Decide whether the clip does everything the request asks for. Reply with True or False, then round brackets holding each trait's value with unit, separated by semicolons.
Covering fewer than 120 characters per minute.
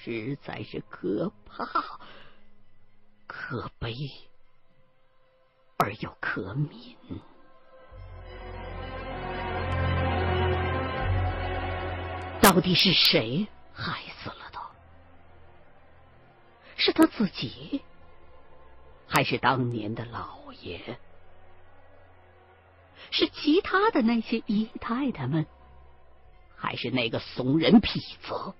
True (100 characters per minute)